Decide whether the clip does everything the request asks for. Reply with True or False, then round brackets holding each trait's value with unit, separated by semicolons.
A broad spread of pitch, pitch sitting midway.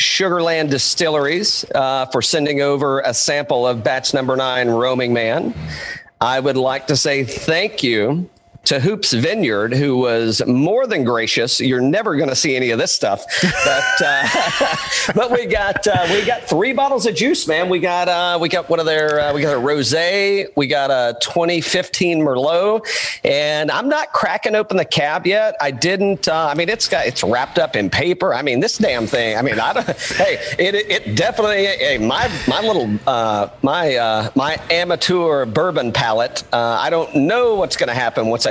True (6.0 semitones; 155 Hz)